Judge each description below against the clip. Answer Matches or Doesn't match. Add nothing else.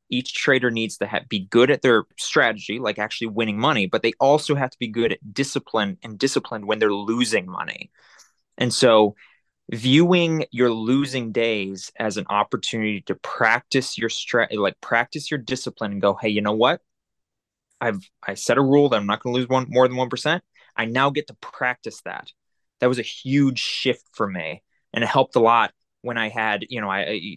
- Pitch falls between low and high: Doesn't match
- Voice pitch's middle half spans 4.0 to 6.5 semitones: Doesn't match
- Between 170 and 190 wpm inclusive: Doesn't match